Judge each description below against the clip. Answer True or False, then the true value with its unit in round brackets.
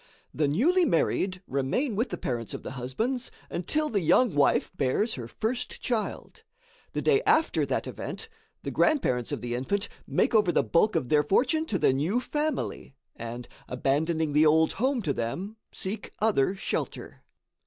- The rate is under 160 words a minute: False (165 wpm)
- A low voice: False (185 Hz)